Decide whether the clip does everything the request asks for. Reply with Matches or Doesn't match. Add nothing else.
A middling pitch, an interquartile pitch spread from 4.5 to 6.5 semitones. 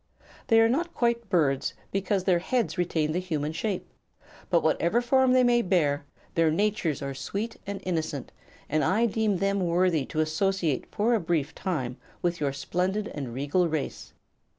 Matches